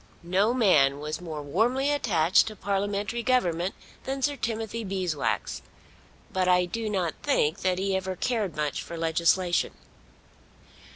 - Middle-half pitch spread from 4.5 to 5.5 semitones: Yes, average, 4.9 semitones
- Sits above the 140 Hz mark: Yes, high, 190 Hz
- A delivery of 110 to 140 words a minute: Yes, slow, 135 wpm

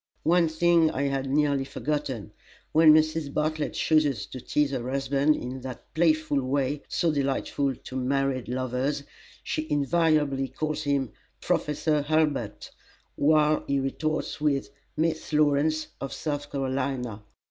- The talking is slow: Yes, slow, 130 wpm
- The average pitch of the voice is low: No, medium, 145 Hz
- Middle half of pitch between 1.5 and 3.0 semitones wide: Yes, narrow, 2.4 semitones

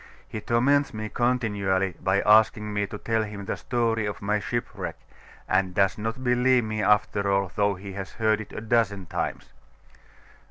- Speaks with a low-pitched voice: Yes, low, 105 Hz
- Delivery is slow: No, average, 170 wpm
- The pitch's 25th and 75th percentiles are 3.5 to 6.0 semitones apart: No, narrow, 2.4 semitones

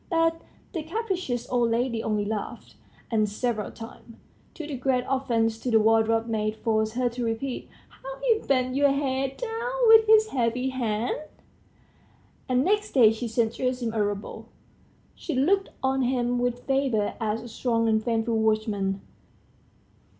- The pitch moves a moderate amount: Yes, average, 3.5 semitones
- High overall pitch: Yes, high, 245 Hz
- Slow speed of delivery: No, average, 155 wpm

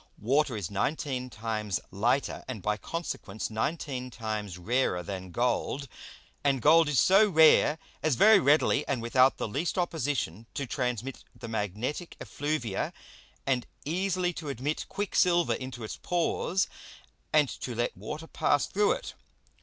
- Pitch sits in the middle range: No, low, 130 Hz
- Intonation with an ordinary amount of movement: No, wide, 5.8 semitones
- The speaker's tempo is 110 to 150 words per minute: Yes, average, 140 wpm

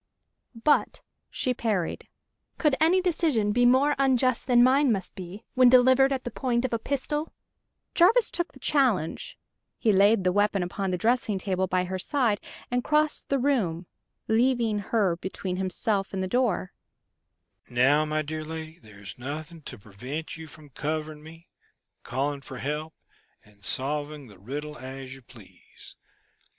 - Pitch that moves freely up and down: Yes, wide, 8.4 semitones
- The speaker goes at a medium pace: Yes, average, 155 wpm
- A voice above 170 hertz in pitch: Yes, high, 190 Hz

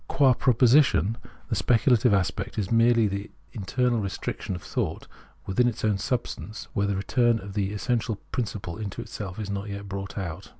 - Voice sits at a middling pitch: No, low, 105 Hz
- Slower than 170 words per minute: No, average, 175 wpm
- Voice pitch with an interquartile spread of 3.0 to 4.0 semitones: Yes, average, 3.3 semitones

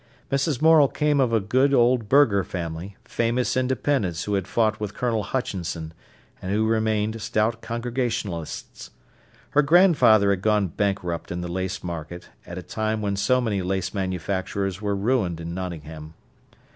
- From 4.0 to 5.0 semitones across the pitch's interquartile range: Yes, average, 4.7 semitones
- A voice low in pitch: Yes, low, 105 Hz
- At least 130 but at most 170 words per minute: Yes, average, 155 wpm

